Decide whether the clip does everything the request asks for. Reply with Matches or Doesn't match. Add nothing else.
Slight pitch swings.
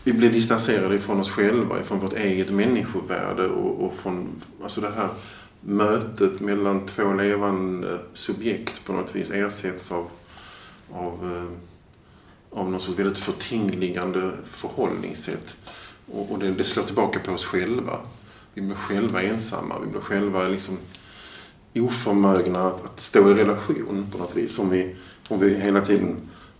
Matches